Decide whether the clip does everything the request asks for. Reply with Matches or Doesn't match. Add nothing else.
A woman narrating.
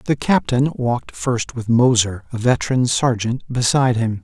Doesn't match